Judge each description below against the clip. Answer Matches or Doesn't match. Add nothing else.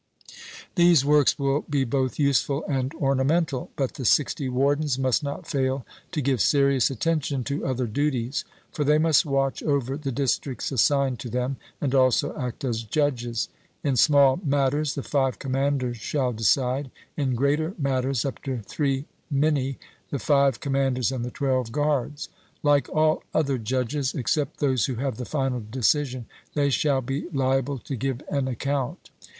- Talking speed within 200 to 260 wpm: Doesn't match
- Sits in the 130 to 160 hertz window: Matches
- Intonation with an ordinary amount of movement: Doesn't match